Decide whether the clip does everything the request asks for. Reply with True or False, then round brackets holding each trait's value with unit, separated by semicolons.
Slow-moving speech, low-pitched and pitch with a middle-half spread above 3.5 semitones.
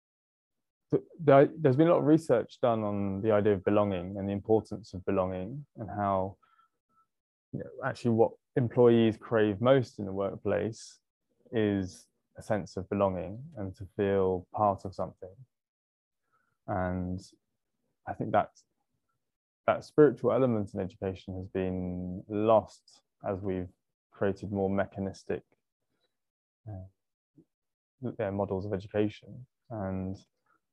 False (125 wpm; 100 Hz; 3.1 semitones)